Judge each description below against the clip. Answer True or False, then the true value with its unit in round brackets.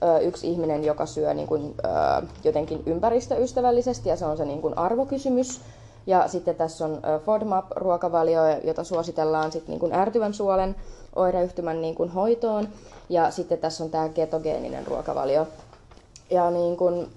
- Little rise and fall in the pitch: False (3.3 semitones)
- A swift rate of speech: False (145 wpm)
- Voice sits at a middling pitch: True (170 Hz)